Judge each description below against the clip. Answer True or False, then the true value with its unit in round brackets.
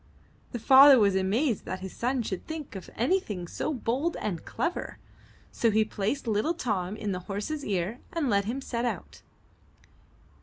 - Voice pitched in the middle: False (225 Hz)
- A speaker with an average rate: True (165 wpm)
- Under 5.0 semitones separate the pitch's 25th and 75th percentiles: False (5.5 semitones)